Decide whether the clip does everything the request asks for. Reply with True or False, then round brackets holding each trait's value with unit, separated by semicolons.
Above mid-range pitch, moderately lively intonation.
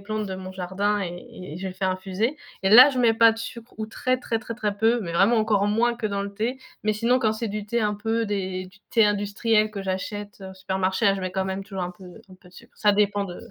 True (205 Hz; 3.0 semitones)